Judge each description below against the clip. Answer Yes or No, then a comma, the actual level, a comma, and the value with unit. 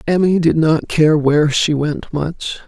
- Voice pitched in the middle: Yes, medium, 155 Hz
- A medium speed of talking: Yes, average, 180 wpm